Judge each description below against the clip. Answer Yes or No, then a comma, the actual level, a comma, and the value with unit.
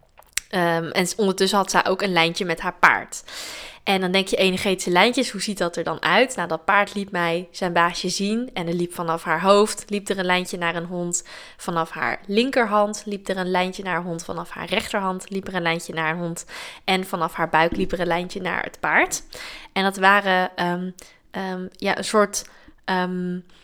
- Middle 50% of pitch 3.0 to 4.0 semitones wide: No, narrow, 2.4 semitones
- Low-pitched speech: No, medium, 185 Hz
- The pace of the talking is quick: Yes, fast, 215 wpm